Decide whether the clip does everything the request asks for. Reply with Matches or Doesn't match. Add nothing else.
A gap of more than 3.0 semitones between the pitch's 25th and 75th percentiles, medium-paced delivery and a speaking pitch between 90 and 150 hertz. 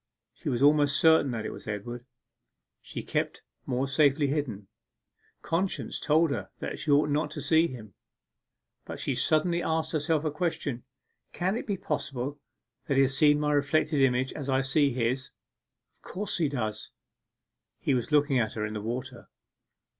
Matches